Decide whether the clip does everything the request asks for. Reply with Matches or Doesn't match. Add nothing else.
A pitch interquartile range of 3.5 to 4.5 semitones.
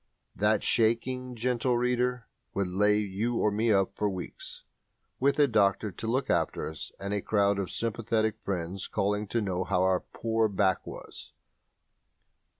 Doesn't match